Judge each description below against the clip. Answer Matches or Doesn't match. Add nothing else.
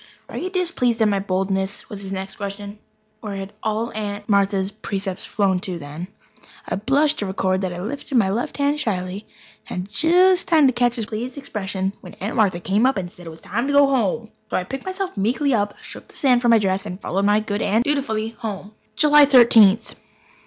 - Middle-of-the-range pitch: Doesn't match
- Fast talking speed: Matches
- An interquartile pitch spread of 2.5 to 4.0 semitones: Doesn't match